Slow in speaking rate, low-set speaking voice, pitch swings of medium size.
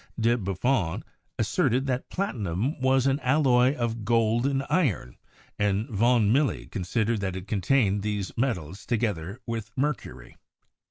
Yes: slow, 130 wpm; low, 115 Hz; average, 4.7 semitones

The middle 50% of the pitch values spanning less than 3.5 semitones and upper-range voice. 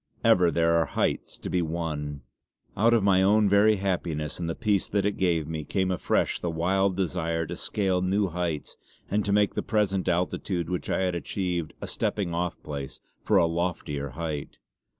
No: average, 2.9 semitones; very low, 90 Hz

